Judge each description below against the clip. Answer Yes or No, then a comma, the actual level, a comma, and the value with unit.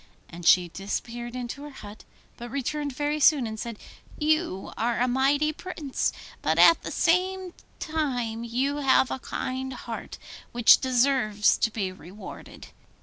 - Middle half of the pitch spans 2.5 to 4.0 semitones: No, average, 4.4 semitones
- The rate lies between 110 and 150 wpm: Yes, average, 145 wpm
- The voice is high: Yes, very high, 255 Hz